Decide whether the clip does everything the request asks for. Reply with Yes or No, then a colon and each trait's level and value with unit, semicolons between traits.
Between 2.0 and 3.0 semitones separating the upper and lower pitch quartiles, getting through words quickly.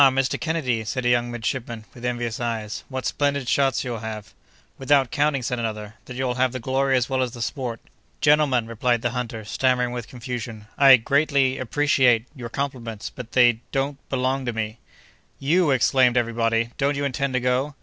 No: narrow, 2.5 semitones; average, 170 wpm